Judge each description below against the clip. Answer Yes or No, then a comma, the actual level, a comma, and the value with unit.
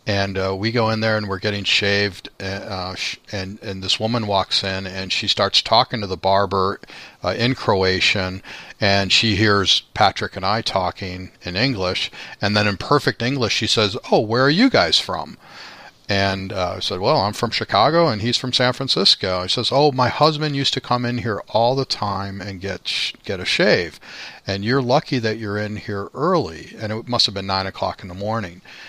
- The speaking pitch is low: Yes, low, 100 Hz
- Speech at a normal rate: No, fast, 210 wpm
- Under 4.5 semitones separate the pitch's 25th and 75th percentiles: Yes, average, 3.7 semitones